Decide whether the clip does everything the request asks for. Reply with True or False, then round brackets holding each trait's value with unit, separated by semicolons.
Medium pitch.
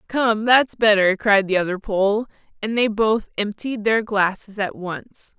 False (220 Hz)